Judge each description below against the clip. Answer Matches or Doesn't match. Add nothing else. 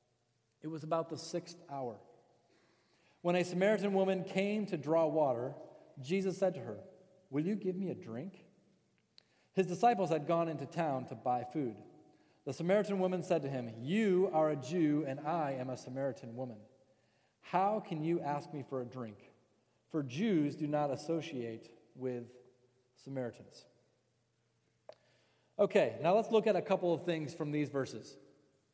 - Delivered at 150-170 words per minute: Matches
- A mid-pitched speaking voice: Matches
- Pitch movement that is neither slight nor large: Doesn't match